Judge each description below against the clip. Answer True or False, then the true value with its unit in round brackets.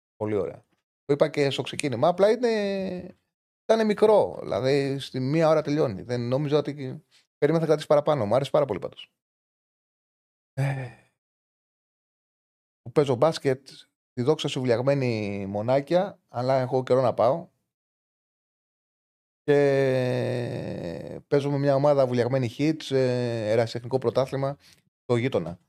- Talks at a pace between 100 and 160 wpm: True (120 wpm)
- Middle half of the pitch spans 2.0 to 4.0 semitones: True (3.5 semitones)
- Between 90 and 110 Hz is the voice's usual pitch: False (135 Hz)